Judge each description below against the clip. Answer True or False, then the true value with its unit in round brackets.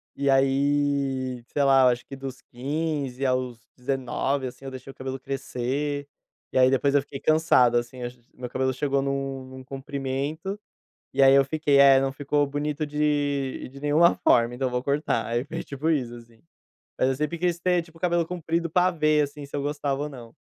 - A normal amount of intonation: False (2.1 semitones)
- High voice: False (140 Hz)